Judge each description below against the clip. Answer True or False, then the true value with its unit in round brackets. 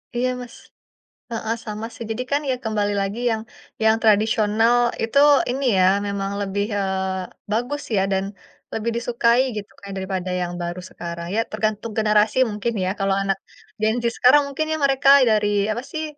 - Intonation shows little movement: False (3.1 semitones)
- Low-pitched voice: False (215 Hz)